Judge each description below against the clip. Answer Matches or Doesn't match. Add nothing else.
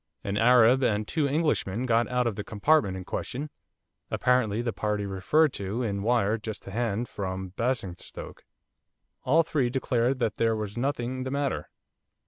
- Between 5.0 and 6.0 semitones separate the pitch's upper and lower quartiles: Doesn't match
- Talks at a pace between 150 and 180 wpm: Matches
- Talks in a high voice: Doesn't match